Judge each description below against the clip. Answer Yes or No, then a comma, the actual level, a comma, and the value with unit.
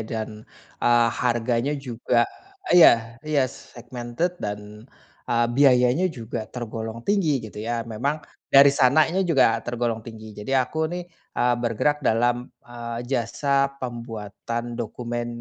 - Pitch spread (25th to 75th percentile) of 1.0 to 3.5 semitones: Yes, narrow, 2.4 semitones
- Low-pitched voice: Yes, low, 120 Hz